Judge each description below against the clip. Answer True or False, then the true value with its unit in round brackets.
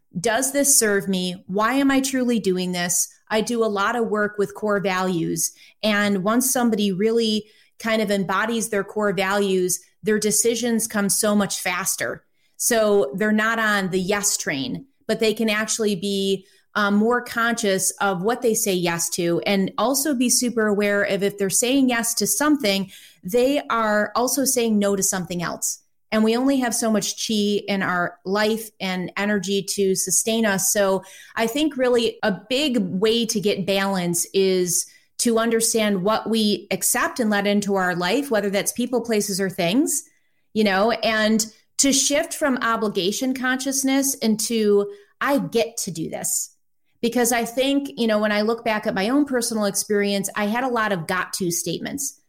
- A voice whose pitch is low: False (215 Hz)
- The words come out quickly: False (175 wpm)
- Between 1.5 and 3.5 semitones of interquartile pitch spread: True (3.0 semitones)